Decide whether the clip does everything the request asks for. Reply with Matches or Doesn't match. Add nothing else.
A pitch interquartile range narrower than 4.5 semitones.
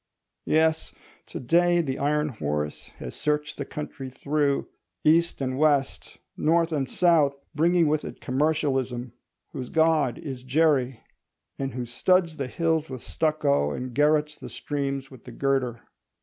Matches